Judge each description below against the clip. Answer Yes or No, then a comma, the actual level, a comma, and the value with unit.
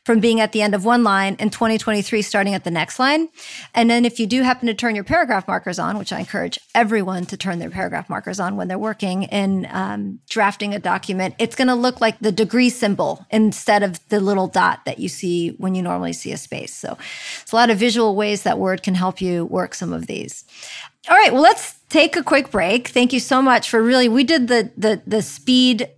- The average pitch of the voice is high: Yes, high, 220 Hz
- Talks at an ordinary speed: No, fast, 235 wpm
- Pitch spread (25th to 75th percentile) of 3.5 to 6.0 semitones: Yes, average, 3.9 semitones